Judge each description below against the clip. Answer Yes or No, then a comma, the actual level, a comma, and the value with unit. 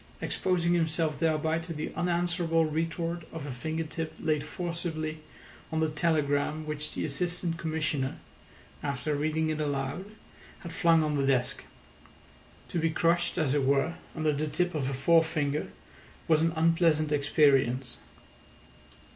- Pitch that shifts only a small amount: Yes, narrow, 2.1 semitones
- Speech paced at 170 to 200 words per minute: No, average, 140 wpm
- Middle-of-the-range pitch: Yes, medium, 155 Hz